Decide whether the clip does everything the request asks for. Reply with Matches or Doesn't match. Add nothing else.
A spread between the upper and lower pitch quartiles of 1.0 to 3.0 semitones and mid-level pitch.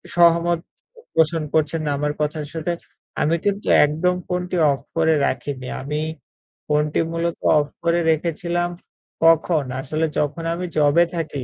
Matches